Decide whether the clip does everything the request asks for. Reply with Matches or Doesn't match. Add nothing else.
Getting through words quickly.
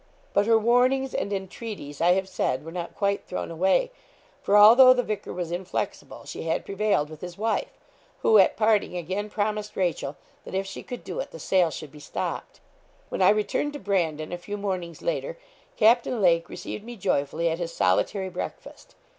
Doesn't match